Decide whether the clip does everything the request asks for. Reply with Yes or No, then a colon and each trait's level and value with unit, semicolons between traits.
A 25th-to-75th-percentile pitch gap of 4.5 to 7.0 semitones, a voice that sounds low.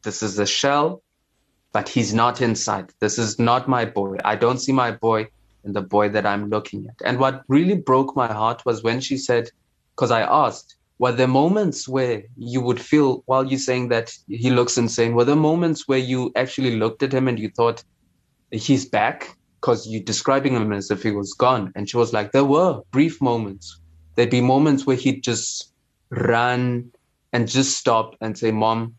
No: average, 3.3 semitones; low, 120 Hz